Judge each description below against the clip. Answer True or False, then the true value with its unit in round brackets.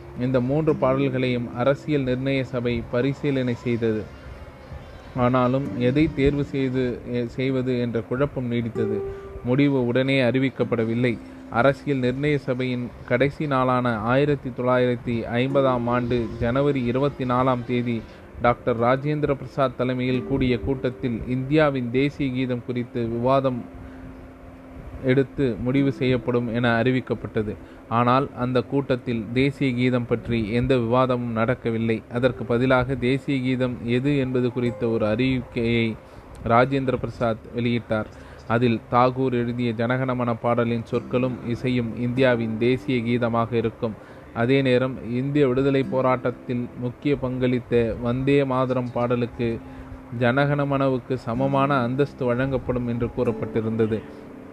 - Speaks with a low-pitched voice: True (125 Hz)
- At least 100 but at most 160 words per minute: True (105 wpm)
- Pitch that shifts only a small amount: True (1.9 semitones)